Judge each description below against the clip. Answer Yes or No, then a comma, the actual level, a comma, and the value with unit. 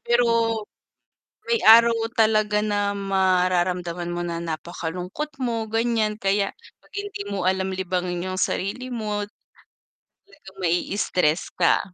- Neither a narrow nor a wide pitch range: Yes, average, 3.7 semitones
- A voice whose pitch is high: Yes, high, 195 Hz